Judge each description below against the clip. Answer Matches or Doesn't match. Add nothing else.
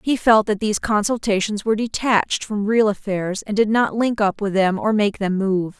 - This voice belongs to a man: Doesn't match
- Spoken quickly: Matches